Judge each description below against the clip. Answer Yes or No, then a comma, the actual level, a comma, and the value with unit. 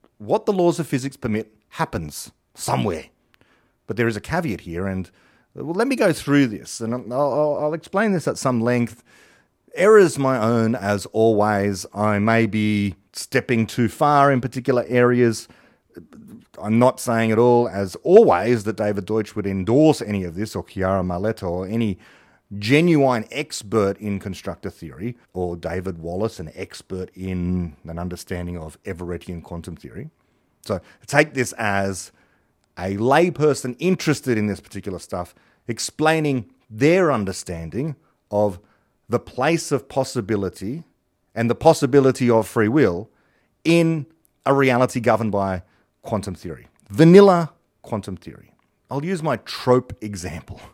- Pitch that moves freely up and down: Yes, wide, 5.8 semitones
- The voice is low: Yes, low, 110 Hz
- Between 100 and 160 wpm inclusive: Yes, average, 145 wpm